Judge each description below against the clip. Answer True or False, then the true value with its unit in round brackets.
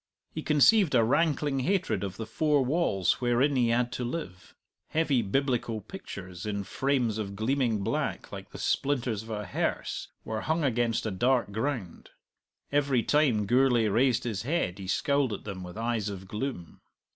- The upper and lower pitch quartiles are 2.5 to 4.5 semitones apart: False (5.1 semitones)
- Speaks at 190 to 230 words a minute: False (170 wpm)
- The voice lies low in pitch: True (120 Hz)